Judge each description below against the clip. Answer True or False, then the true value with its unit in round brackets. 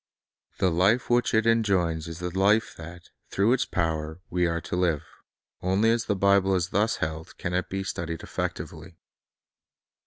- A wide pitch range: False (3.6 semitones)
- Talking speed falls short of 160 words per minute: False (165 wpm)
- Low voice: True (90 Hz)